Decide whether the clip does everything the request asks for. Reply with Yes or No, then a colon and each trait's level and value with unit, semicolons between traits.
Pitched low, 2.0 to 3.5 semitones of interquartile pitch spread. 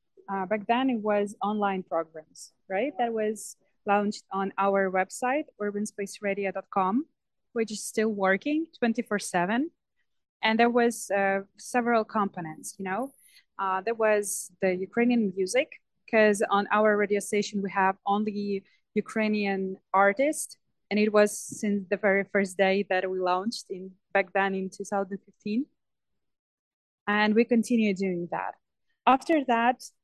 No: high, 205 Hz; average, 2.9 semitones